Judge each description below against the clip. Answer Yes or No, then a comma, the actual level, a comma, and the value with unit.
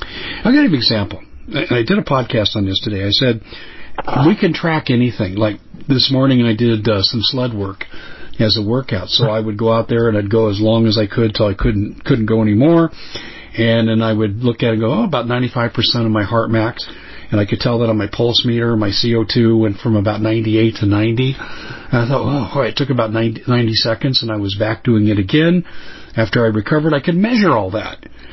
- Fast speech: Yes, fast, 235 wpm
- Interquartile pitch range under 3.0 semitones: Yes, narrow, 2.6 semitones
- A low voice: Yes, low, 115 Hz